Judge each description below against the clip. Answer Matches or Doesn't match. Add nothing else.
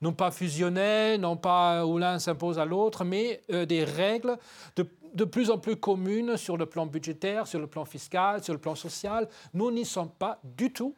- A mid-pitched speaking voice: Matches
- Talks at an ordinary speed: Matches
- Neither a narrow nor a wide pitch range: Matches